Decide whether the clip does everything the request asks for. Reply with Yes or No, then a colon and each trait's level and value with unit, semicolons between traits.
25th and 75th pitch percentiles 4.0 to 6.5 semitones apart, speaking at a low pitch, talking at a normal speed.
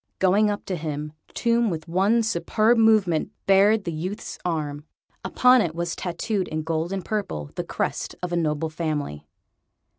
No: average, 5.0 semitones; medium, 175 Hz; average, 160 wpm